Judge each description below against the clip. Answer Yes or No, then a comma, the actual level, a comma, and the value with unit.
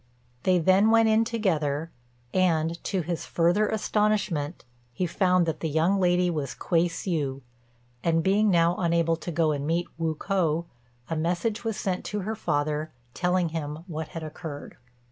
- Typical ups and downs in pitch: Yes, average, 3.1 semitones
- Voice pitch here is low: No, medium, 170 Hz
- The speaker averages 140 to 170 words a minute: Yes, average, 165 wpm